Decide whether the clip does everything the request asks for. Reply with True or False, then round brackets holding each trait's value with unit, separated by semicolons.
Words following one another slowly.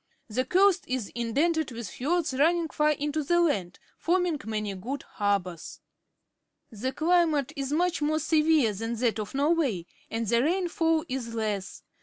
False (150 wpm)